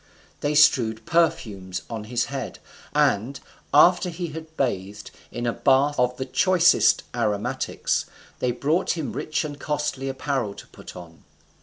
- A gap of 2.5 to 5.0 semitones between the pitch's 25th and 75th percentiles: No, wide, 5.5 semitones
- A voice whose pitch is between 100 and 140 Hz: Yes, low, 135 Hz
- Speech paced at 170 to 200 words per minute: No, average, 145 wpm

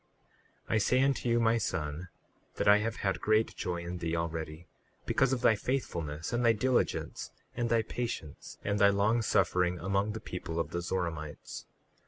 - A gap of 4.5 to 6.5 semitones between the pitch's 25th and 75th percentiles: Yes, average, 5.2 semitones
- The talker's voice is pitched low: Yes, low, 100 Hz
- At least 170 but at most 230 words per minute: Yes, average, 180 wpm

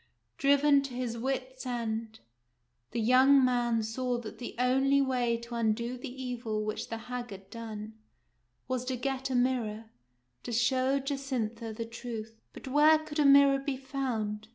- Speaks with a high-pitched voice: Yes, high, 245 Hz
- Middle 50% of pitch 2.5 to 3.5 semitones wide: Yes, average, 2.8 semitones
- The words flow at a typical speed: Yes, average, 160 wpm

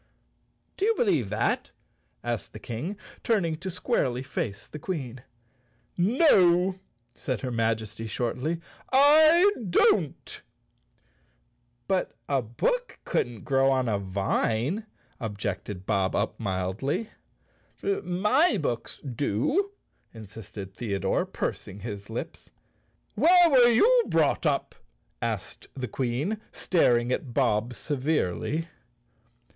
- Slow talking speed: Yes, slow, 110 wpm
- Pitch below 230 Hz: Yes, low, 135 Hz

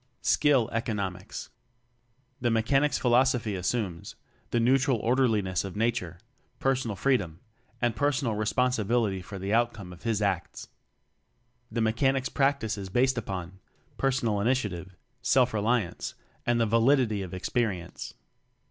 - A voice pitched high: No, low, 115 Hz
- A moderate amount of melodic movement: Yes, average, 4.3 semitones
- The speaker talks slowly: Yes, slow, 130 wpm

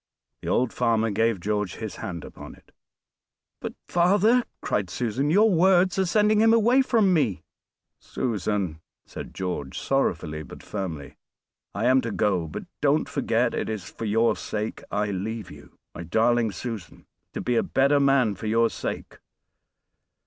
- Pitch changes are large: Yes, wide, 6.7 semitones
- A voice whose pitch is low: Yes, low, 115 Hz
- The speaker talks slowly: No, average, 155 wpm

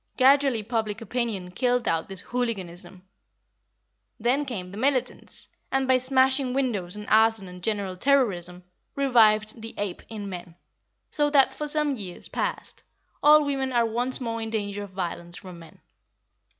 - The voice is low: No, high, 225 Hz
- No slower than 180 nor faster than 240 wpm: No, average, 150 wpm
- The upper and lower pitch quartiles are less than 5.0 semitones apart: No, wide, 5.4 semitones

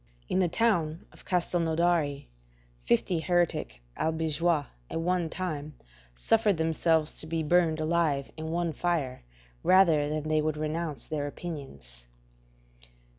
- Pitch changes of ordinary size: No, narrow, 2.3 semitones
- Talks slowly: Yes, slow, 125 wpm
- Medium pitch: Yes, medium, 160 Hz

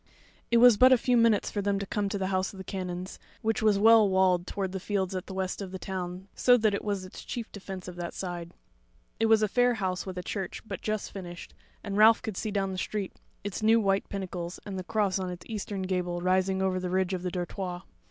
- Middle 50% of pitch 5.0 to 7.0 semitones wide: No, narrow, 2.4 semitones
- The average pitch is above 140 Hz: Yes, high, 190 Hz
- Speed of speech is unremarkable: No, fast, 250 wpm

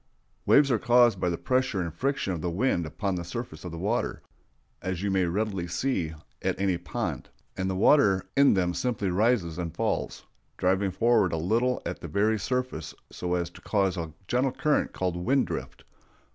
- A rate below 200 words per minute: Yes, average, 190 wpm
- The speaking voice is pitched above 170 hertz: No, very low, 95 Hz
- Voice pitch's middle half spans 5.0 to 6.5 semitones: Yes, wide, 5.4 semitones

